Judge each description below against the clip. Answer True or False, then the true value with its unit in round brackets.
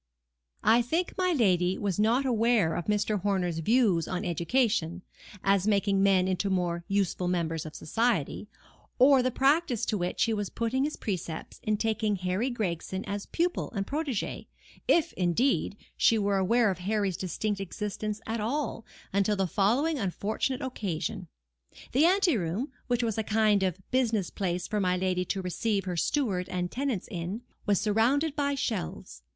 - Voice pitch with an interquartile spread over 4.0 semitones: True (4.7 semitones)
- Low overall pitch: False (205 Hz)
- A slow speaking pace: False (160 wpm)